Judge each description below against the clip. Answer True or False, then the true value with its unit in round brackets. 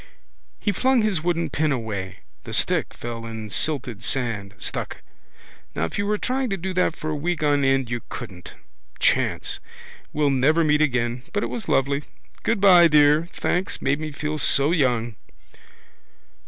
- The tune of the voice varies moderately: False (6.1 semitones)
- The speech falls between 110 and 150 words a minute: False (165 wpm)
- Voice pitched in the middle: True (145 Hz)